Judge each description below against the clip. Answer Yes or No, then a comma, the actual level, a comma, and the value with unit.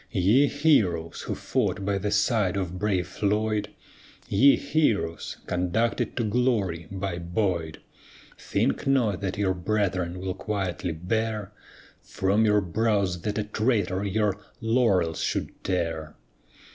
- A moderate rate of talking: No, slow, 125 wpm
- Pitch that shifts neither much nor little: Yes, average, 3.3 semitones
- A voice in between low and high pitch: No, low, 100 Hz